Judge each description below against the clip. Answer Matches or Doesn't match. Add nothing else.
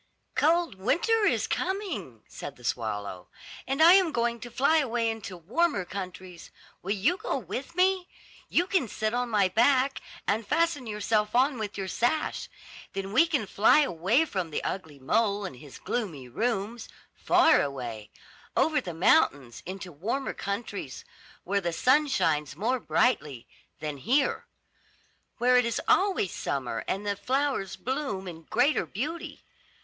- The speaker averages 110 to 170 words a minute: Matches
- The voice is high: Matches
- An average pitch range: Doesn't match